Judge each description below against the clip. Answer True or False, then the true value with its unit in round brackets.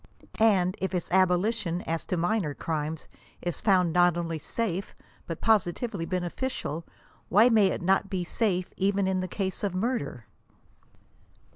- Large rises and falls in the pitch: False (2.8 semitones)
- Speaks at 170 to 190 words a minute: False (155 wpm)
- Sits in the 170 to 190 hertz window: True (185 Hz)